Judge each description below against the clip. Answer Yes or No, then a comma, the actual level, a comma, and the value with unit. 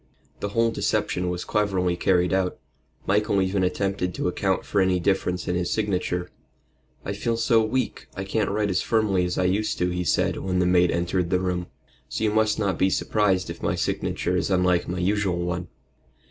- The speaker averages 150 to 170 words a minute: No, average, 195 wpm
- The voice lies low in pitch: Yes, very low, 95 Hz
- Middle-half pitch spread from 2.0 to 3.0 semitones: Yes, narrow, 2.4 semitones